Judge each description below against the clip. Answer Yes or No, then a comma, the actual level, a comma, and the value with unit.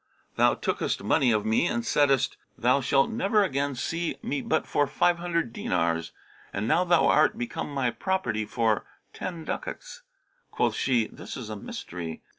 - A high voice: No, medium, 140 Hz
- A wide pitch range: Yes, wide, 7.3 semitones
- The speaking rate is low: No, average, 165 wpm